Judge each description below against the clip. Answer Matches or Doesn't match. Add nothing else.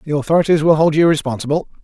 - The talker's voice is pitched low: Doesn't match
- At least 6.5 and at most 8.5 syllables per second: Matches